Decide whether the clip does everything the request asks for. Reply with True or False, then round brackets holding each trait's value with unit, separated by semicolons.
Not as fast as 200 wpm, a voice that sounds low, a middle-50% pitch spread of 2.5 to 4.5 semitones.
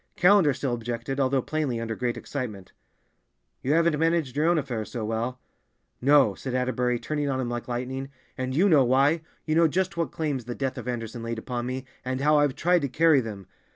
False (205 wpm; 130 Hz; 3.8 semitones)